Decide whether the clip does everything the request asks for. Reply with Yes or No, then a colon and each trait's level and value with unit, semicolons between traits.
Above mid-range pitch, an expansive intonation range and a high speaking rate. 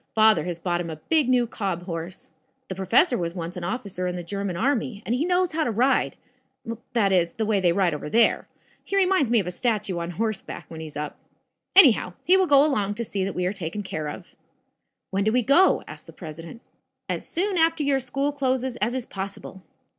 Yes: high, 210 Hz; wide, 6.6 semitones; fast, 220 wpm